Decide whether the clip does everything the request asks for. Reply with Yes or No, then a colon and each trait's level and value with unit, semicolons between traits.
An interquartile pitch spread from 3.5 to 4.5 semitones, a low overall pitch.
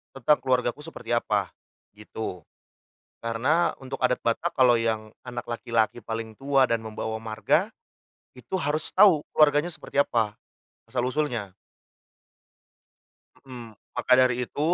Yes: average, 4.0 semitones; low, 125 Hz